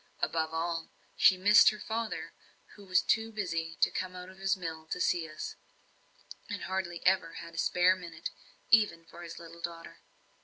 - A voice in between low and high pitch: Yes, medium, 180 Hz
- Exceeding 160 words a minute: Yes, average, 170 wpm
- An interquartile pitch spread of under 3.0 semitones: Yes, narrow, 2.5 semitones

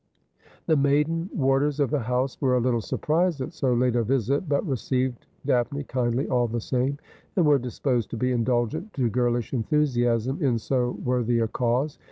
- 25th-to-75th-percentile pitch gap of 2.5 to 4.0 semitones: Yes, average, 2.8 semitones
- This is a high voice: No, low, 125 Hz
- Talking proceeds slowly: No, average, 180 wpm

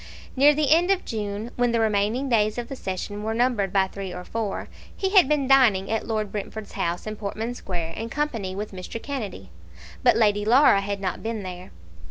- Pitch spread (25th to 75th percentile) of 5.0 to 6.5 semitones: No, average, 3.7 semitones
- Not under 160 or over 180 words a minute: No, fast, 205 wpm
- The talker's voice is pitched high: Yes, high, 215 Hz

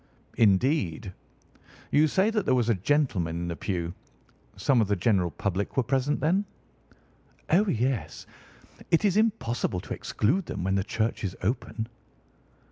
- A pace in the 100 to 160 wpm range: Yes, average, 150 wpm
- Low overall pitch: Yes, low, 115 Hz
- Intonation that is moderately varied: No, wide, 7.7 semitones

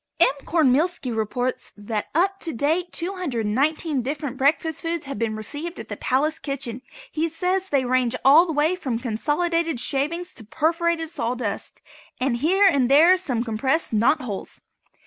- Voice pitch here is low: No, very high, 290 Hz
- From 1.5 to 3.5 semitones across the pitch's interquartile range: No, average, 5.2 semitones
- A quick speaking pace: No, average, 155 wpm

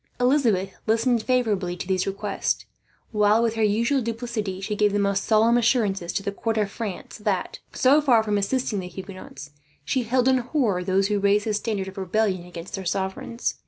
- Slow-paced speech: No, average, 190 wpm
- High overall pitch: Yes, high, 210 Hz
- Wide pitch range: No, average, 3.3 semitones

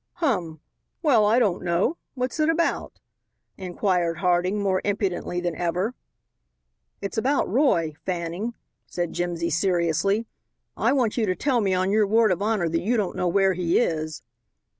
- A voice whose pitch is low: No, high, 190 Hz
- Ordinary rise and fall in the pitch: Yes, average, 4.2 semitones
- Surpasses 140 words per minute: Yes, average, 160 wpm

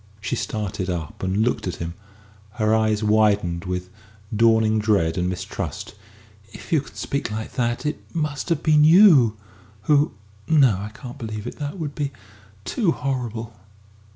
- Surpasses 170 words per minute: No, average, 165 wpm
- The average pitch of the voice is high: No, low, 110 Hz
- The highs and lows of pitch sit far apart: Yes, wide, 5.7 semitones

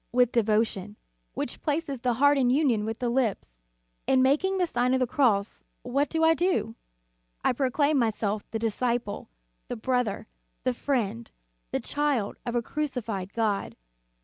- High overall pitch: Yes, high, 245 Hz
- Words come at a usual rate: Yes, average, 155 wpm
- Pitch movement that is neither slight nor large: Yes, average, 4.4 semitones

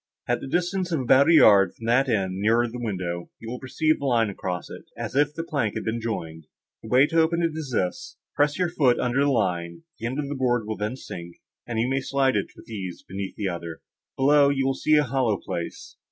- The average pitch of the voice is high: No, low, 120 Hz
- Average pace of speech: No, fast, 235 wpm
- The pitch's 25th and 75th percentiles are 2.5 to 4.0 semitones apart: No, wide, 5.6 semitones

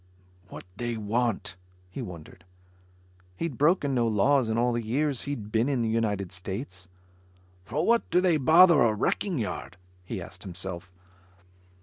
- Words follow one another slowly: No, average, 150 wpm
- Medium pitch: No, low, 115 Hz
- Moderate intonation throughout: No, wide, 5.9 semitones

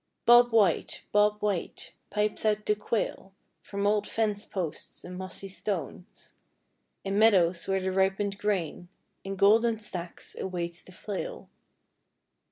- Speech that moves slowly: Yes, slow, 130 wpm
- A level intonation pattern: Yes, narrow, 2.1 semitones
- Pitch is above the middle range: Yes, high, 200 Hz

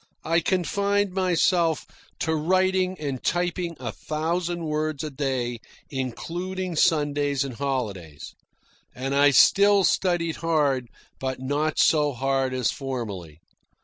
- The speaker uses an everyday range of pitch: Yes, average, 4.7 semitones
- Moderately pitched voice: Yes, medium, 150 Hz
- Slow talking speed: Yes, slow, 115 wpm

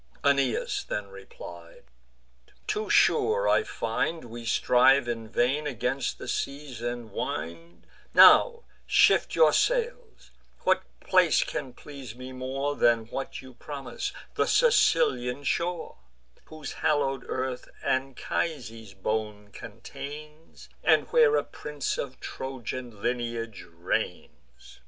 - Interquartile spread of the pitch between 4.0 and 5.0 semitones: Yes, average, 4.5 semitones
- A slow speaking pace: Yes, slow, 115 wpm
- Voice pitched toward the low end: Yes, low, 130 Hz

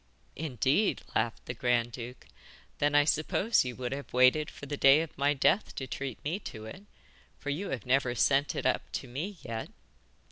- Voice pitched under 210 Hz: Yes, low, 135 Hz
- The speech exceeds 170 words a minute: Yes, average, 190 wpm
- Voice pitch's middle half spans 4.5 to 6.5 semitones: No, average, 3.4 semitones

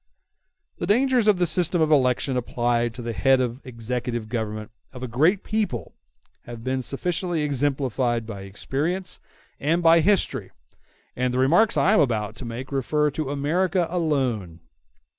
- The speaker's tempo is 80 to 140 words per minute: No, average, 160 wpm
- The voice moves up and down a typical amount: No, wide, 6.0 semitones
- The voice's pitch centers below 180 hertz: Yes, low, 135 Hz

